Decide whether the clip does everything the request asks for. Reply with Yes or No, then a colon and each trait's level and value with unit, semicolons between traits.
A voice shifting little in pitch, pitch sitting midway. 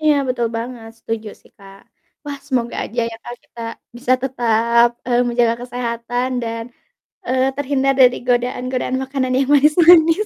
No: narrow, 2.2 semitones; high, 245 Hz